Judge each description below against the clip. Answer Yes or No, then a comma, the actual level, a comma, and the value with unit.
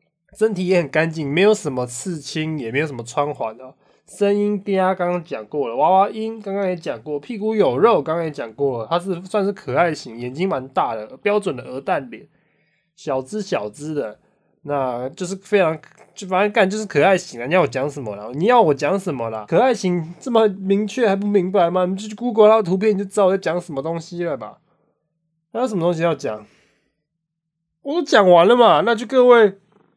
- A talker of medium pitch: Yes, medium, 175 Hz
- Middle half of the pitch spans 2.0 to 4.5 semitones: No, average, 5.2 semitones